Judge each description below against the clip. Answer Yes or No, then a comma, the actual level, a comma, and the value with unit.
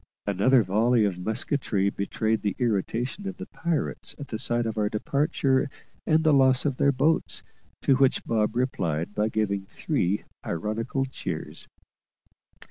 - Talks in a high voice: No, low, 115 Hz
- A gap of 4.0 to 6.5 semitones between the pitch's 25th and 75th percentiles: Yes, average, 4.5 semitones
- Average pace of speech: Yes, average, 145 wpm